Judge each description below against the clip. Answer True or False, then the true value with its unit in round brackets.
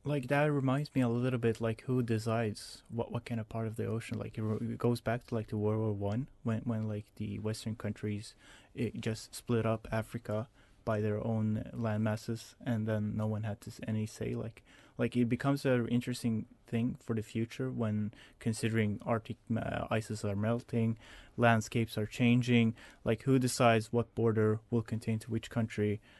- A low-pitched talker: True (115 Hz)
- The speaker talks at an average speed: True (190 wpm)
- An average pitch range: False (1.7 semitones)